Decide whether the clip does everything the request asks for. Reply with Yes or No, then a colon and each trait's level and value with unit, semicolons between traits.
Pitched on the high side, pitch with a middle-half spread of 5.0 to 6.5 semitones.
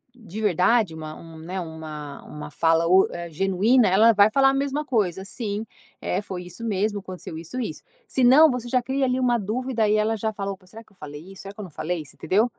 Yes: high, 200 Hz; wide, 5.4 semitones